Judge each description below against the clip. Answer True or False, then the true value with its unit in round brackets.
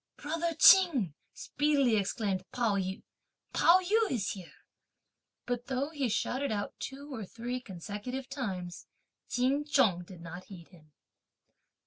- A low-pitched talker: False (245 Hz)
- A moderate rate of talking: False (130 wpm)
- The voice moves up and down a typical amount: False (6.7 semitones)